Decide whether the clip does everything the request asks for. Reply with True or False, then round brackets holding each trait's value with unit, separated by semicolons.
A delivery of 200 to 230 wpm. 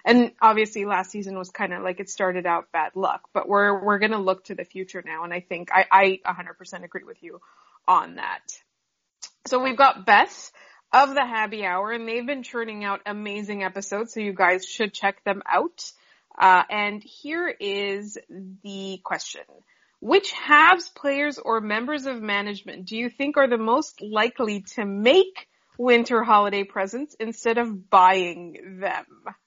False (170 wpm)